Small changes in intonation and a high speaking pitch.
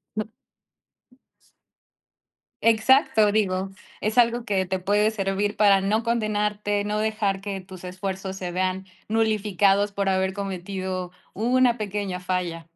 Yes: narrow, 2.2 semitones; high, 200 Hz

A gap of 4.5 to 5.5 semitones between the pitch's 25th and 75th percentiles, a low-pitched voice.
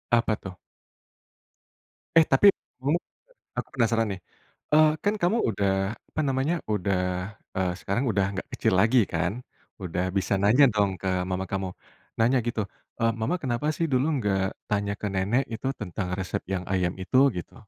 Yes: average, 5.2 semitones; low, 105 Hz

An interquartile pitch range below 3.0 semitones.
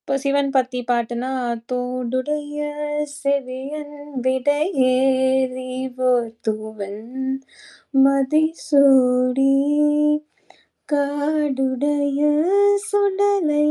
Yes: narrow, 2.5 semitones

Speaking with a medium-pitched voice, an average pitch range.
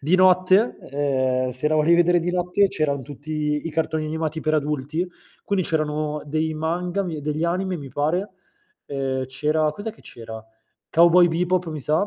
Yes: medium, 155 Hz; average, 3.1 semitones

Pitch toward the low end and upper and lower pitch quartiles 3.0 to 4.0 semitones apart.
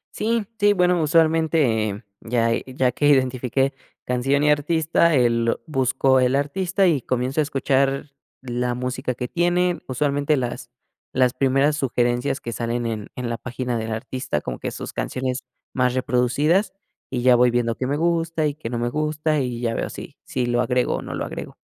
Yes: low, 130 Hz; average, 3.6 semitones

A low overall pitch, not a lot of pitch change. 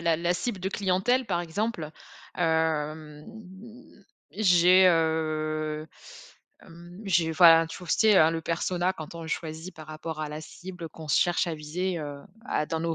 No: medium, 165 Hz; narrow, 2.3 semitones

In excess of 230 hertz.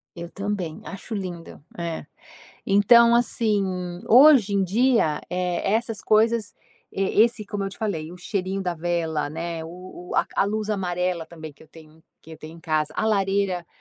No: medium, 185 Hz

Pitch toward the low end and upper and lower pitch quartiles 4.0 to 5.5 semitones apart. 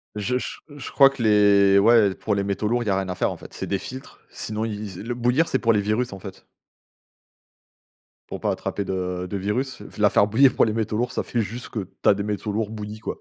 No: low, 105 Hz; average, 2.9 semitones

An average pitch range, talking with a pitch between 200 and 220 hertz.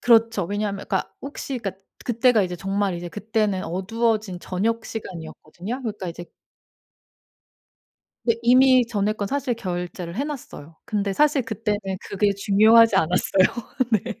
Yes: average, 3.5 semitones; high, 210 Hz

